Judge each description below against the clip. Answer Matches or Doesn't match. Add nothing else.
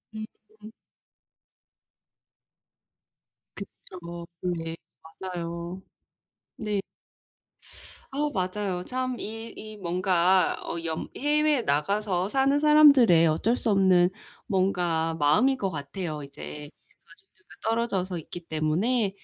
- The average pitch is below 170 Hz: Doesn't match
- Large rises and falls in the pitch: Doesn't match